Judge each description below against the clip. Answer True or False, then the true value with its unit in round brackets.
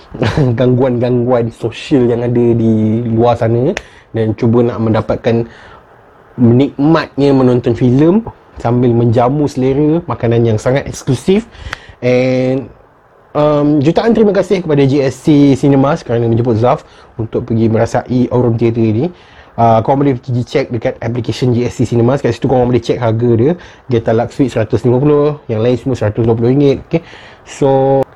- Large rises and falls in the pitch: False (2.9 semitones)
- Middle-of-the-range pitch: False (125 Hz)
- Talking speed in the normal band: True (135 wpm)